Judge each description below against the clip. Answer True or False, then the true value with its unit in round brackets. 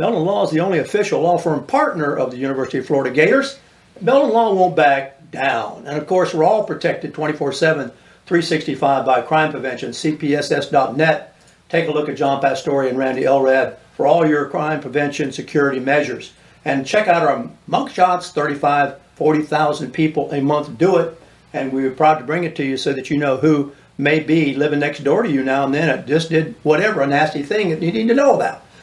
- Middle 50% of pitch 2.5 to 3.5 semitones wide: True (3.1 semitones)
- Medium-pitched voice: True (150 Hz)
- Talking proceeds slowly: False (200 wpm)